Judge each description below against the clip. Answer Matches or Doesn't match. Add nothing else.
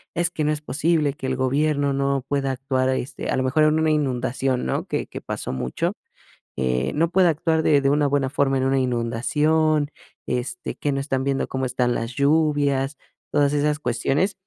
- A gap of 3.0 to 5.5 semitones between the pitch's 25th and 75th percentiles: Doesn't match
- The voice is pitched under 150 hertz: Matches